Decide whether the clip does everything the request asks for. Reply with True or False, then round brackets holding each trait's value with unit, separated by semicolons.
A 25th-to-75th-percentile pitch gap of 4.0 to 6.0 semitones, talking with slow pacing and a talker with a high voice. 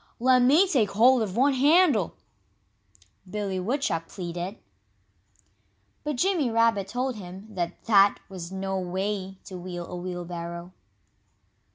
True (5.5 semitones; 125 wpm; 200 Hz)